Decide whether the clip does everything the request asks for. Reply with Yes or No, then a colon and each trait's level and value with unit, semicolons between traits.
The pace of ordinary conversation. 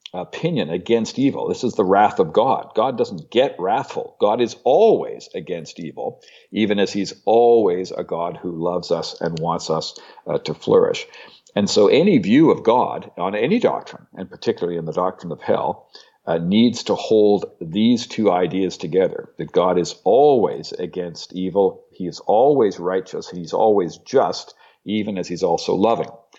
Yes: average, 170 wpm